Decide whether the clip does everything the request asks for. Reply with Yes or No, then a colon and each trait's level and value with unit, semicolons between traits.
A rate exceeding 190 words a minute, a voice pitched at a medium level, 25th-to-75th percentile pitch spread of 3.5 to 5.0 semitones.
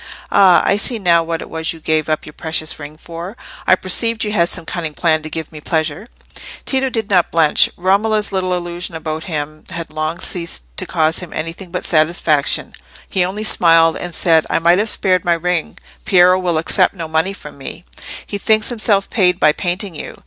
No: average, 200 wpm; medium, 170 Hz; average, 3.0 semitones